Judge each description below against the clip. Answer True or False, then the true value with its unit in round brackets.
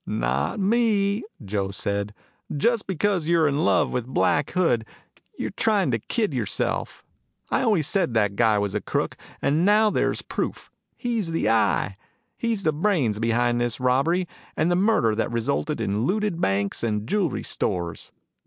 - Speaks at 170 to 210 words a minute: False (160 wpm)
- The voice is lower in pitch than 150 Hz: True (140 Hz)